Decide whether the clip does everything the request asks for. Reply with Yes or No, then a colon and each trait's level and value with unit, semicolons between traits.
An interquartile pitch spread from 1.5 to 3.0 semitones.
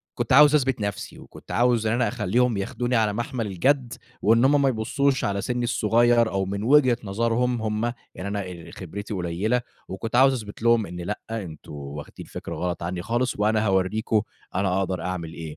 No: average, 4.2 semitones